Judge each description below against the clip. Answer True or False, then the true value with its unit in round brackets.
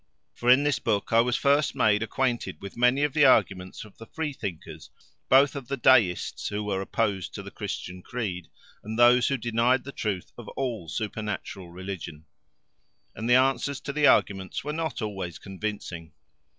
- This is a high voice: False (115 Hz)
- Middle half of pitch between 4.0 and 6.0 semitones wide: True (5.3 semitones)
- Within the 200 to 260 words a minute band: False (175 wpm)